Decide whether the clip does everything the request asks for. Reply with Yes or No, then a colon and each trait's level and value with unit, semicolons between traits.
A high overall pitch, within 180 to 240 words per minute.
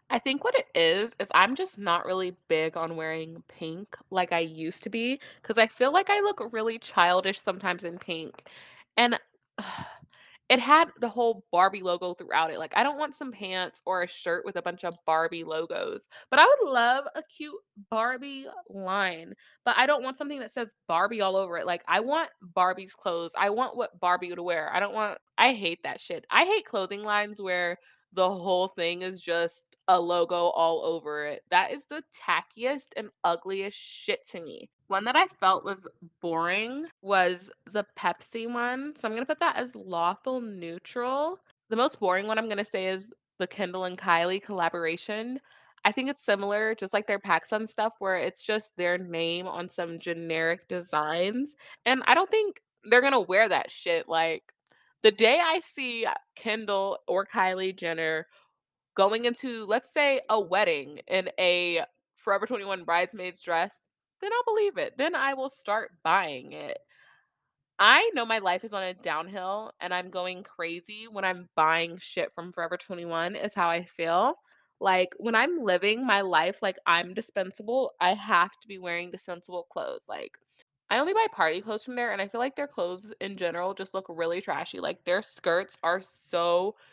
Yes: high, 195 Hz; average, 185 wpm